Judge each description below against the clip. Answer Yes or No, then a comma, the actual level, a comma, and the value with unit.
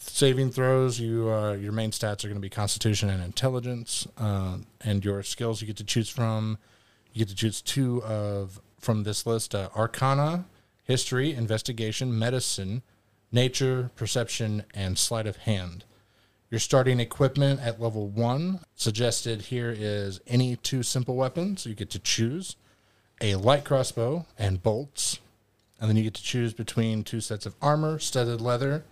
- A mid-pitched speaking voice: No, low, 115 Hz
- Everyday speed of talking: Yes, average, 165 wpm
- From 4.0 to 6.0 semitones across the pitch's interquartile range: No, average, 3.2 semitones